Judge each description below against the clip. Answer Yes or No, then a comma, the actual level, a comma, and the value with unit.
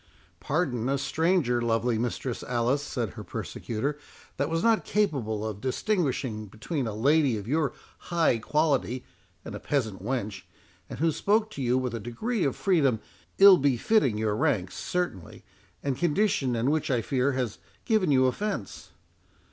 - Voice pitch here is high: No, low, 130 Hz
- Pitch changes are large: Yes, wide, 5.7 semitones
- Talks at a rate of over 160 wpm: No, average, 155 wpm